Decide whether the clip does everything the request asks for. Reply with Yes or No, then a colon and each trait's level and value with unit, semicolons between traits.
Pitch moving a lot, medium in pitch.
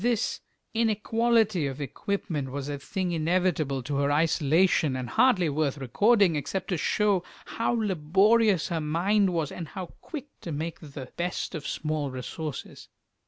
Yes: wide, 5.7 semitones; medium, 165 Hz